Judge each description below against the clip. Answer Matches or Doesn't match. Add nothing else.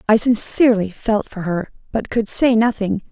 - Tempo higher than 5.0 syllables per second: Doesn't match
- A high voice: Matches